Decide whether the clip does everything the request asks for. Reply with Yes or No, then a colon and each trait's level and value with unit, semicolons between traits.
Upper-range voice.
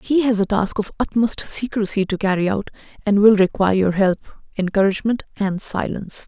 Yes: high, 205 Hz